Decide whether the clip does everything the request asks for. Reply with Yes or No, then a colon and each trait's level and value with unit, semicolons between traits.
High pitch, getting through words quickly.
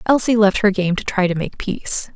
Yes: high, 200 Hz; fast, 250 wpm